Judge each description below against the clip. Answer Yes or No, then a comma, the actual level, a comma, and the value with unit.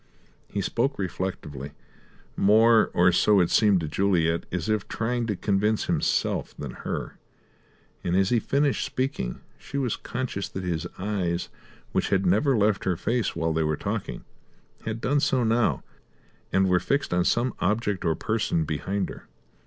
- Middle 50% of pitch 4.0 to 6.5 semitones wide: Yes, average, 4.5 semitones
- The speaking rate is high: No, average, 160 wpm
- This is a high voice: No, low, 100 Hz